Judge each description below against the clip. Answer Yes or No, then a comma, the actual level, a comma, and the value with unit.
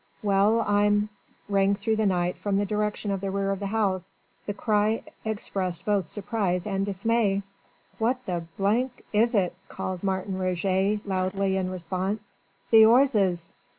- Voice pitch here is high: Yes, high, 200 Hz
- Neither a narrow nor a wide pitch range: No, narrow, 2.1 semitones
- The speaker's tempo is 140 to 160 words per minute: Yes, average, 150 wpm